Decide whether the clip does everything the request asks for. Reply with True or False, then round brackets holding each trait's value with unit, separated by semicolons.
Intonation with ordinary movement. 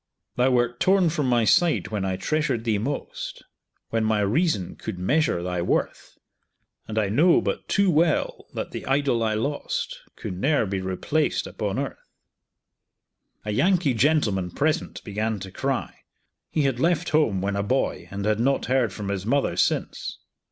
False (6.8 semitones)